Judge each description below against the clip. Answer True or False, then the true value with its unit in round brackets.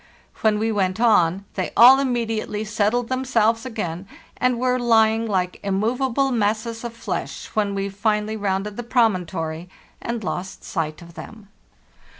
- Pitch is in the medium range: False (220 Hz)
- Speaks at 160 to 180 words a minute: False (145 wpm)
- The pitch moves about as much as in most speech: True (3.2 semitones)